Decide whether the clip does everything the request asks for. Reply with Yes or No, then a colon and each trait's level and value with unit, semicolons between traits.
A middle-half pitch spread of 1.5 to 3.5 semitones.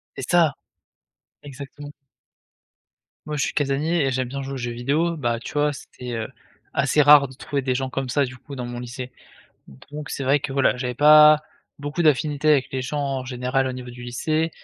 Yes: narrow, 2.6 semitones